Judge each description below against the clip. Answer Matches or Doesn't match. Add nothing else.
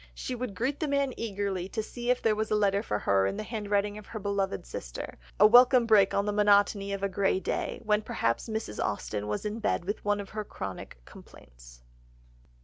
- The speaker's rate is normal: Doesn't match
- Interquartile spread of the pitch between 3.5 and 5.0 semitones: Doesn't match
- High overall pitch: Matches